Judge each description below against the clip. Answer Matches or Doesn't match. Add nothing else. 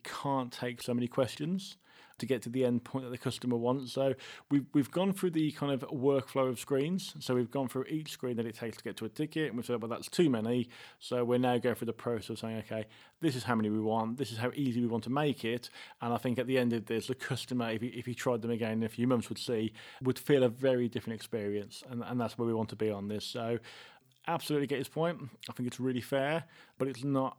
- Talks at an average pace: Doesn't match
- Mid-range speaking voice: Doesn't match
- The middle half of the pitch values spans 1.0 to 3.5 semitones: Matches